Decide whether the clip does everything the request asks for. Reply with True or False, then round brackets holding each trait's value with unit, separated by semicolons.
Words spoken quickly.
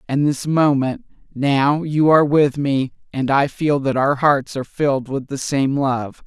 False (190 wpm)